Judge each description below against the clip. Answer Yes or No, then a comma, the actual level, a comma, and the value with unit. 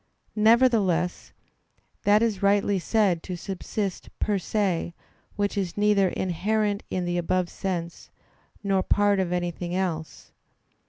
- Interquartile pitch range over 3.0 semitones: No, average, 2.7 semitones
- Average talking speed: No, slow, 120 wpm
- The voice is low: No, high, 190 Hz